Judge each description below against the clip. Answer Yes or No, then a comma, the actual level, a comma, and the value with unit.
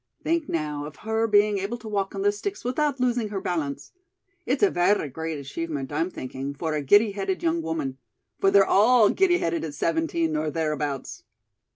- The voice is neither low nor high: Yes, medium, 170 Hz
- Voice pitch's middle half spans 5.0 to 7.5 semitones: Yes, wide, 5.6 semitones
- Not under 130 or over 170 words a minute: No, average, 190 wpm